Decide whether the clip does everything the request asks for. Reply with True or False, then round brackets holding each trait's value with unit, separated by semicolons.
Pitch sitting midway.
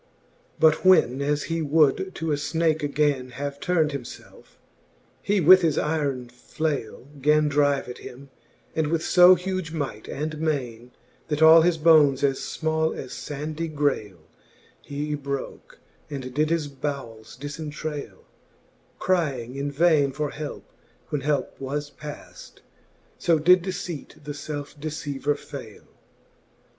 True (150 Hz)